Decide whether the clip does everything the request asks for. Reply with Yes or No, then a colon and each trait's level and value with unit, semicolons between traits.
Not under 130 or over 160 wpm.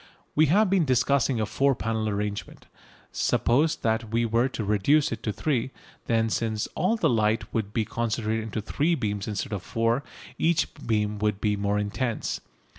No: average, 175 wpm